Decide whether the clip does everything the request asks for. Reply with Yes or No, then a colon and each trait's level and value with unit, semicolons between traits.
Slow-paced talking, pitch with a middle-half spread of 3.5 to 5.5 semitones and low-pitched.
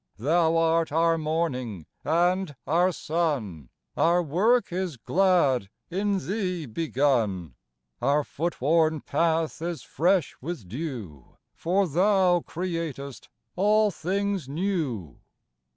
No: slow, 105 wpm; average, 4.6 semitones; medium, 165 Hz